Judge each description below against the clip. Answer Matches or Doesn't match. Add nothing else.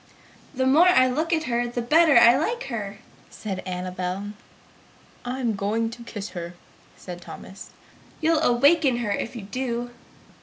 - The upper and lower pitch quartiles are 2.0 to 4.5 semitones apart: Doesn't match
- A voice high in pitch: Matches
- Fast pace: Doesn't match